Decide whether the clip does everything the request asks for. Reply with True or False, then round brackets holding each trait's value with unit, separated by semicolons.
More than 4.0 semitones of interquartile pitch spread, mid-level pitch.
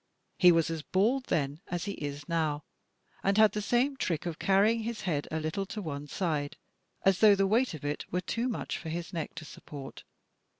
True (5.2 semitones; 175 Hz)